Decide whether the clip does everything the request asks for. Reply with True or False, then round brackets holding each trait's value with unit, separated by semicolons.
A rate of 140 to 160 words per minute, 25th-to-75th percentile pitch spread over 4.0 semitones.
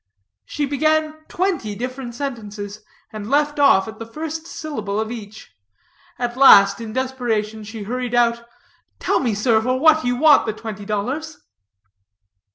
True (150 wpm; 4.8 semitones)